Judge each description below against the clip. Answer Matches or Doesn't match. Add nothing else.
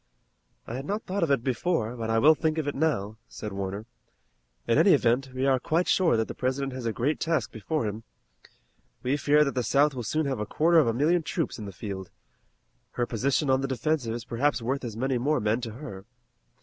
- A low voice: Matches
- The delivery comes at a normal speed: Doesn't match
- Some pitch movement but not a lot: Matches